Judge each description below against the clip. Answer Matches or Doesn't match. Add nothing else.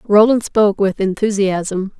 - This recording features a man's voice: Doesn't match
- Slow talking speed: Matches